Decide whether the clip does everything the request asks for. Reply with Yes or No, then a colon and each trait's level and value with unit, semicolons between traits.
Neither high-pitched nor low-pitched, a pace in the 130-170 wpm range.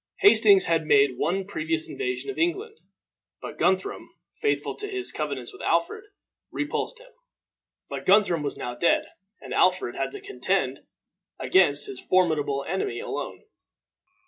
No: high, 195 Hz; average, 140 wpm